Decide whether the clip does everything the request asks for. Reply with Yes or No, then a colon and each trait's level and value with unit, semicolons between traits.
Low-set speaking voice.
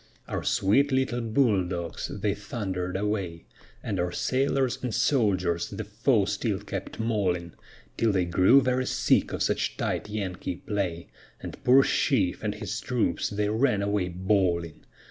Yes: low, 100 Hz